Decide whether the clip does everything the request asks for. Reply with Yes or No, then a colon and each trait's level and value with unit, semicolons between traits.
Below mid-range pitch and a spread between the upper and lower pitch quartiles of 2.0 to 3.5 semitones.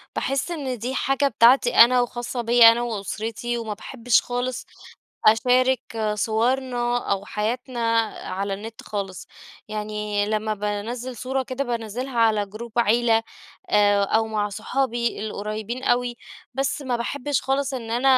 No: high, 235 Hz; average, 2.9 semitones